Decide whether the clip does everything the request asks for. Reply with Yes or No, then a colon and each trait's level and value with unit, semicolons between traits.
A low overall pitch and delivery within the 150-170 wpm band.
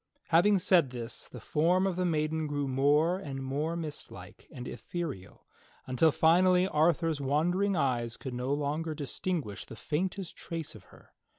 No: medium, 155 Hz; average, 160 wpm